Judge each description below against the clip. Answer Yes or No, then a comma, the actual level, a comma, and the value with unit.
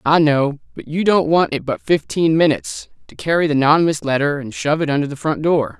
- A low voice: No, medium, 155 Hz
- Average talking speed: No, fast, 230 wpm